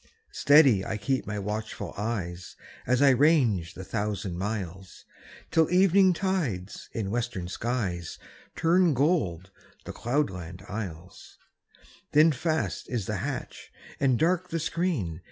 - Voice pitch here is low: Yes, low, 115 Hz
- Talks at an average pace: No, slow, 125 wpm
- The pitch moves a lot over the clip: Yes, wide, 8.7 semitones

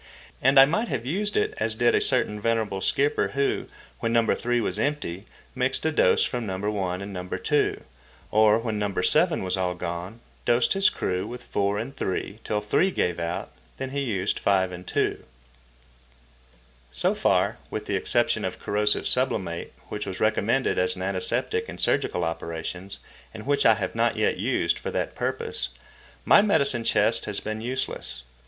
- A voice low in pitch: Yes, low, 110 Hz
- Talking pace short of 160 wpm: No, average, 175 wpm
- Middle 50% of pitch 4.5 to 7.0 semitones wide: Yes, average, 5.0 semitones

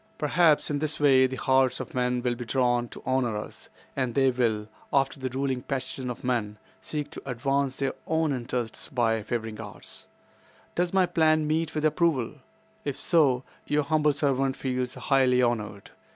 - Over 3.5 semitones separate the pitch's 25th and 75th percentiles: No, average, 3.2 semitones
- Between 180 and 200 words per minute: No, average, 165 wpm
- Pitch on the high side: No, low, 130 Hz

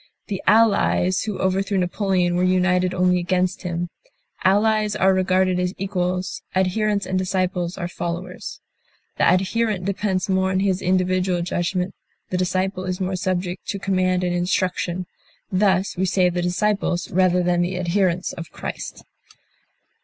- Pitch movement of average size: No, narrow, 1.1 semitones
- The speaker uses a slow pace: No, average, 145 wpm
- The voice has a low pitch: No, medium, 185 Hz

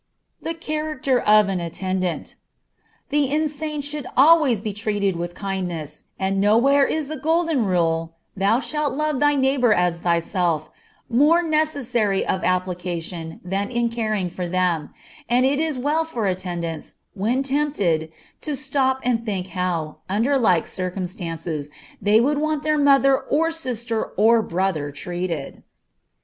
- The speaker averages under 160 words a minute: Yes, average, 140 wpm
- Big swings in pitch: Yes, wide, 7.8 semitones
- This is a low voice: No, high, 215 Hz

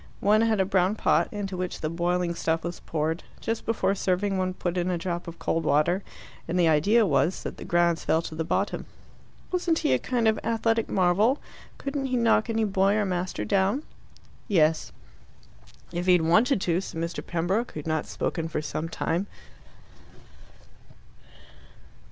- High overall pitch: No, medium, 180 Hz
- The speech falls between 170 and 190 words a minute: Yes, average, 175 wpm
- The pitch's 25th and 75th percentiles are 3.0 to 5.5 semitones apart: Yes, average, 4.2 semitones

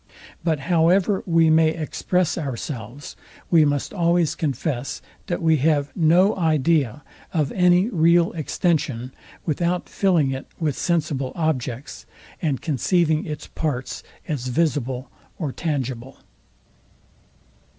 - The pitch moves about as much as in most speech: Yes, average, 3.8 semitones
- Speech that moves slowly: Yes, slow, 110 wpm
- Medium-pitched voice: Yes, medium, 155 Hz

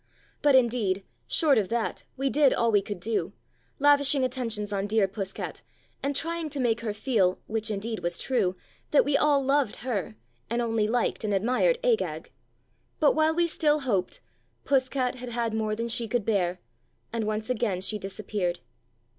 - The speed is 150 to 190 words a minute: Yes, average, 180 wpm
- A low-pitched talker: No, high, 230 Hz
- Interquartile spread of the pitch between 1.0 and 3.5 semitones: No, average, 4.7 semitones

